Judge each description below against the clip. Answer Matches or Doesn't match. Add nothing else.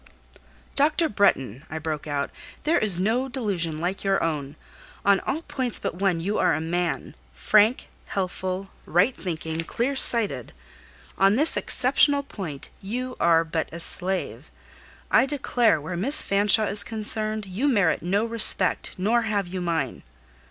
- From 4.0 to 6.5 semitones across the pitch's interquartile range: Matches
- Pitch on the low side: Doesn't match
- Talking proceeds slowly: Doesn't match